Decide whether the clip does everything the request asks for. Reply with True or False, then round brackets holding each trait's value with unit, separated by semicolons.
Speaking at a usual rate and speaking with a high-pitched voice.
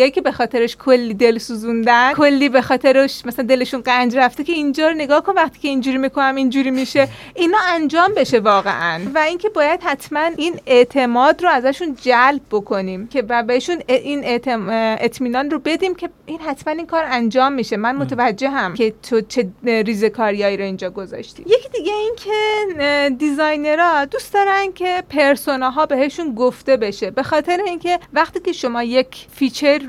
False (170 wpm; 270 Hz)